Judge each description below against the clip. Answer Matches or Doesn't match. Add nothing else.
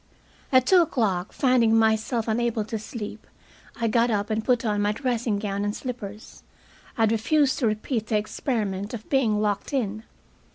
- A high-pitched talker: Matches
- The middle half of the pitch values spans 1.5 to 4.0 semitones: Matches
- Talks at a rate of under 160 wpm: Doesn't match